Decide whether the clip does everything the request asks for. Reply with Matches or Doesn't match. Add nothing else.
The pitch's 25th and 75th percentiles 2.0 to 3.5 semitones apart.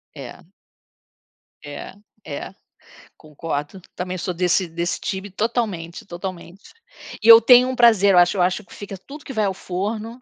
Doesn't match